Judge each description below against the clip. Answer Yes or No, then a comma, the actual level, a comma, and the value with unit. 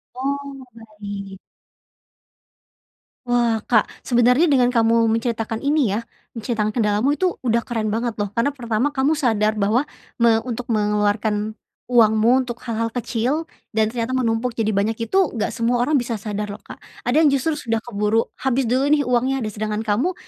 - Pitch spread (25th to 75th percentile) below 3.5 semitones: Yes, average, 2.8 semitones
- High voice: Yes, high, 230 Hz